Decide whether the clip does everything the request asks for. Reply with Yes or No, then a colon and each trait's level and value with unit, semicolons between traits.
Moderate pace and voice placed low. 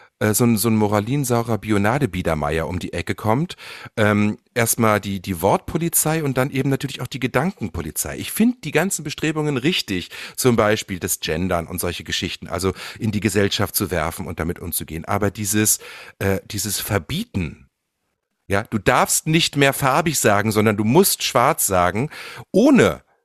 Yes: average, 160 wpm; low, 105 Hz